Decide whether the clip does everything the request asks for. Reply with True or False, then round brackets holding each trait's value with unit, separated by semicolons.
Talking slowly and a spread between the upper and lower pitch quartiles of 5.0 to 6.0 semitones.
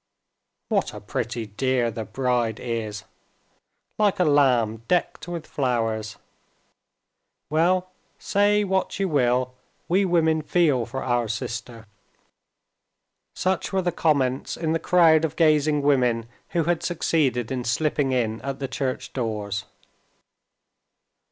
True (120 wpm; 5.5 semitones)